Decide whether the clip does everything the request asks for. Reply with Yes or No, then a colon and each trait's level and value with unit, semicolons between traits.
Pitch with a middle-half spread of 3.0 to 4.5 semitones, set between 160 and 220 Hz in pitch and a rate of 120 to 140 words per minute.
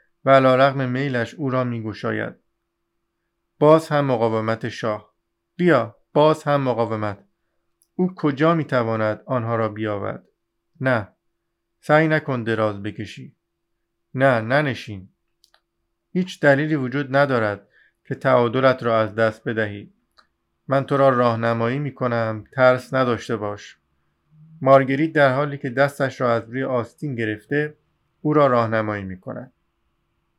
No: average, 4.2 semitones; low, 125 Hz; average, 125 wpm